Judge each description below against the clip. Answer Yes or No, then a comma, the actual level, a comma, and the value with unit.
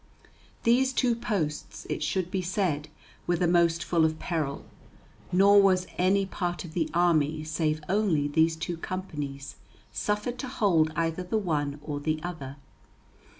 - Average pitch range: Yes, average, 3.6 semitones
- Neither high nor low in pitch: Yes, medium, 170 Hz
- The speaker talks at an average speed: Yes, average, 150 wpm